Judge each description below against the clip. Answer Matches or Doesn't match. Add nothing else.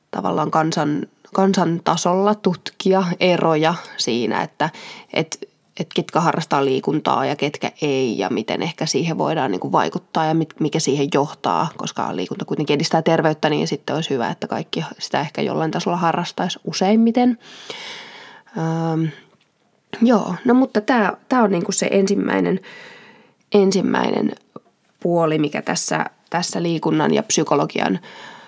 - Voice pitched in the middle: Matches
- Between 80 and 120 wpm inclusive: Doesn't match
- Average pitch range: Matches